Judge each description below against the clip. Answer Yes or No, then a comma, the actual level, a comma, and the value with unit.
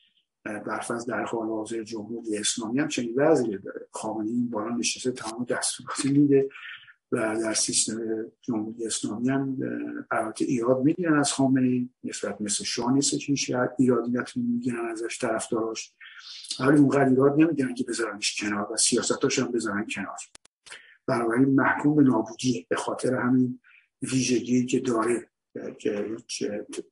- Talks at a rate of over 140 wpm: No, average, 135 wpm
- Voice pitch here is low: Yes, low, 125 Hz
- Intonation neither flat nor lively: Yes, average, 3.2 semitones